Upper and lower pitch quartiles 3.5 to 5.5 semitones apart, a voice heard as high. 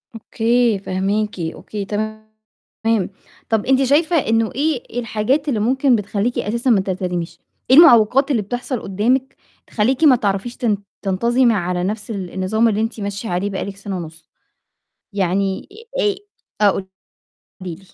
Yes: average, 3.8 semitones; high, 215 Hz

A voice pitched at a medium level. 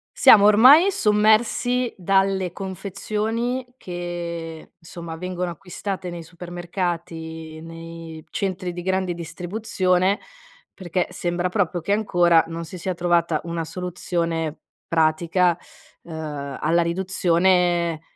Yes: medium, 175 Hz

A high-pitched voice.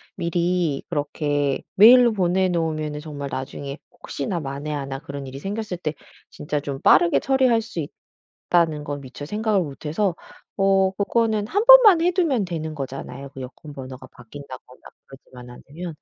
No: medium, 155 Hz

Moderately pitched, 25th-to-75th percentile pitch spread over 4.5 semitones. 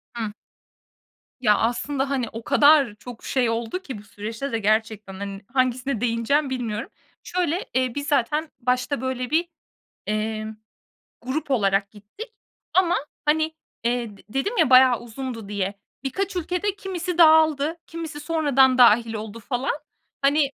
No: very high, 255 Hz; average, 5.1 semitones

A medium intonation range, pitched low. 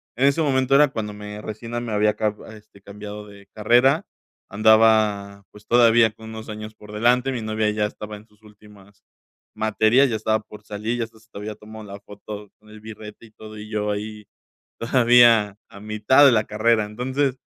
No: narrow, 1.7 semitones; low, 110 Hz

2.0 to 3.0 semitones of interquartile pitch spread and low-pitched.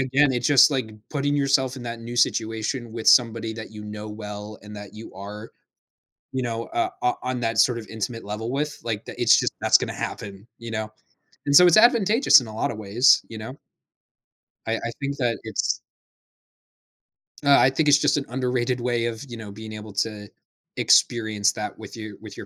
No: average, 3.4 semitones; low, 115 Hz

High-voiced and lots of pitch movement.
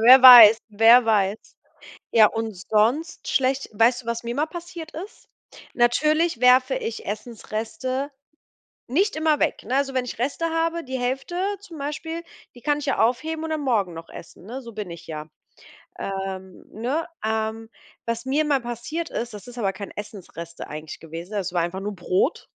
Yes: high, 240 Hz; wide, 5.8 semitones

